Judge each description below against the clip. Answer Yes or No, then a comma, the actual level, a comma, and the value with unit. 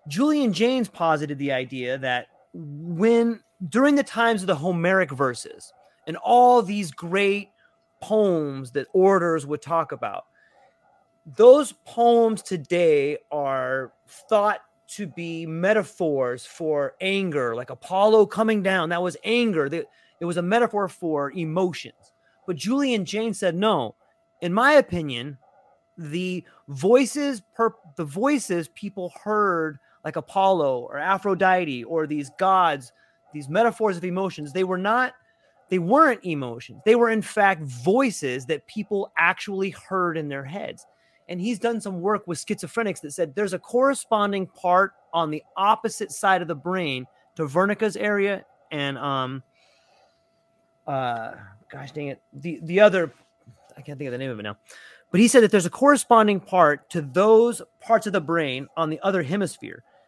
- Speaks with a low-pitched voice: No, medium, 185 Hz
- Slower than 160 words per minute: Yes, average, 150 wpm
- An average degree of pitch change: No, wide, 5.7 semitones